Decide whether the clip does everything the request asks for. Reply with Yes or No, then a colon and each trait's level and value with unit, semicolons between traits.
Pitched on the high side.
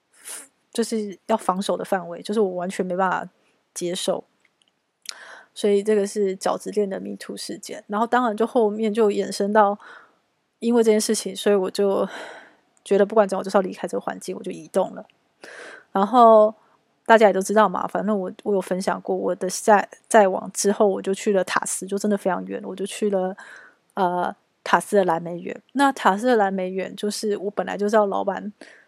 Yes: high, 205 Hz